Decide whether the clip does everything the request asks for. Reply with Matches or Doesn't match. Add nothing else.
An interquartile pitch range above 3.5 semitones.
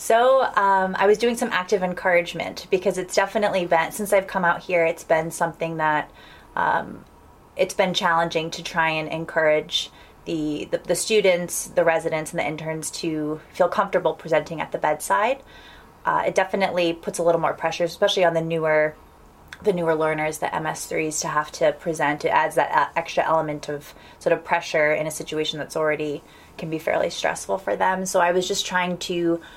Doesn't match